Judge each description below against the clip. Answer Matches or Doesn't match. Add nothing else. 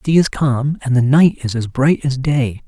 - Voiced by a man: Matches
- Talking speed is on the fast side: Matches